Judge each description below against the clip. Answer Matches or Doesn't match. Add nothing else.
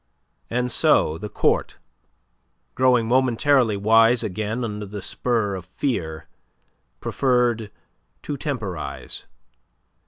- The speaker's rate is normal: Doesn't match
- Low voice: Matches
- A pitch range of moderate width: Matches